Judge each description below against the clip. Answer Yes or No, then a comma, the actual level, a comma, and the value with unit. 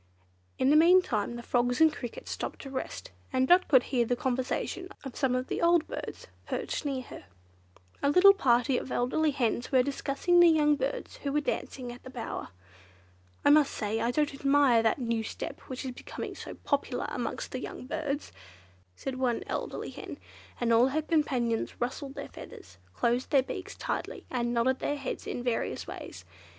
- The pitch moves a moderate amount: Yes, average, 3.1 semitones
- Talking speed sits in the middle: Yes, average, 185 wpm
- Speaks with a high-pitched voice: Yes, very high, 260 Hz